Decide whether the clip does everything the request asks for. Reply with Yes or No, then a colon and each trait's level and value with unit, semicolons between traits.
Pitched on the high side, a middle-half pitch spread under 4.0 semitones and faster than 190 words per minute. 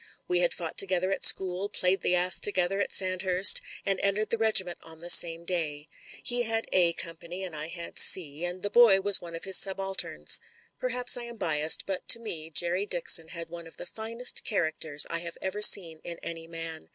No: medium, 180 Hz; average, 2.9 semitones; fast, 205 wpm